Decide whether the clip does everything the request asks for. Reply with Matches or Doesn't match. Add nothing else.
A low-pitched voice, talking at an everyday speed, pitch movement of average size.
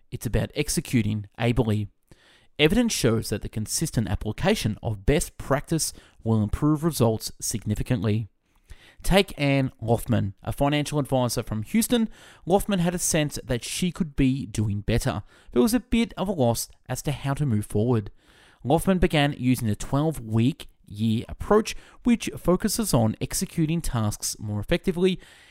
Doesn't match